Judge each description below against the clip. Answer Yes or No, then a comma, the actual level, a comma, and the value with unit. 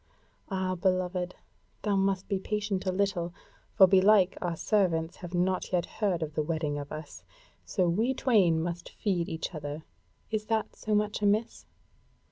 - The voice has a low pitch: No, medium, 185 Hz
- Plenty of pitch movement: No, average, 3.1 semitones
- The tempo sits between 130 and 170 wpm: Yes, average, 165 wpm